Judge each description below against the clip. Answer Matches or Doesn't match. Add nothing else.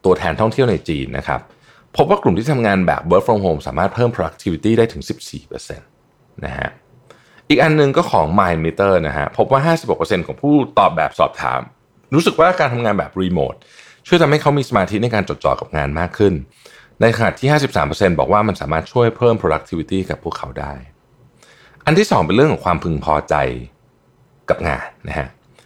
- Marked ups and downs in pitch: Matches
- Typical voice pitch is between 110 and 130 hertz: Doesn't match